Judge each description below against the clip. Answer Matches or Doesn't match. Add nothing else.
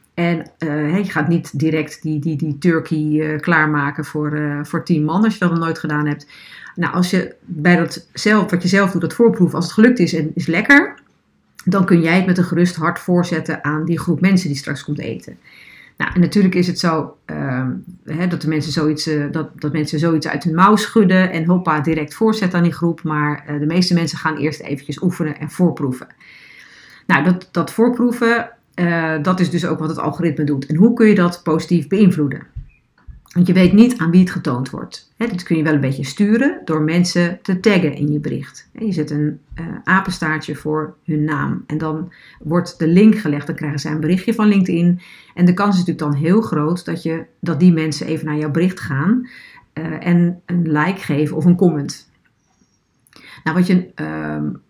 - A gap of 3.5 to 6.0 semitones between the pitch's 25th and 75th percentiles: Doesn't match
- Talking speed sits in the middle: Doesn't match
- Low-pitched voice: Doesn't match